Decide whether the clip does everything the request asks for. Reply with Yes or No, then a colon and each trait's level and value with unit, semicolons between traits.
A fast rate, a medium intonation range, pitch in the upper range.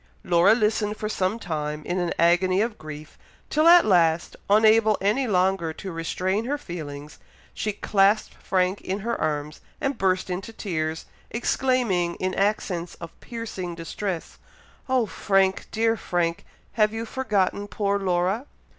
No: average, 145 wpm; average, 4.0 semitones; high, 195 Hz